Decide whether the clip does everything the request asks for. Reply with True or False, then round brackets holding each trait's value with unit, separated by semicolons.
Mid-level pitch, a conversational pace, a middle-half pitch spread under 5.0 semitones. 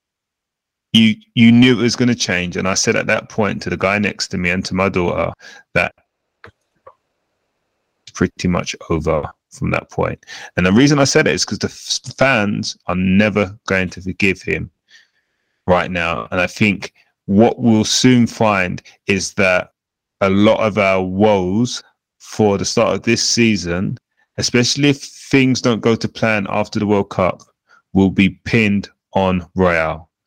False (100 Hz; 170 wpm; 4.0 semitones)